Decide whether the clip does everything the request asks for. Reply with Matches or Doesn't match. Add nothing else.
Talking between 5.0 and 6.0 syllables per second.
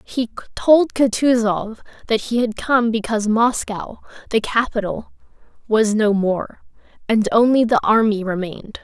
Doesn't match